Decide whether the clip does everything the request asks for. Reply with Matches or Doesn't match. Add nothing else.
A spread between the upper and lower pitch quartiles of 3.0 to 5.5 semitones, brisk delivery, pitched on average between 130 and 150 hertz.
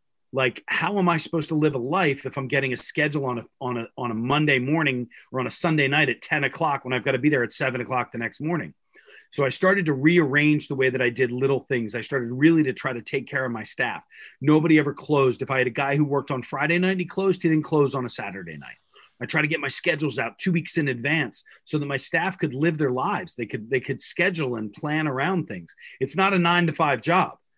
Matches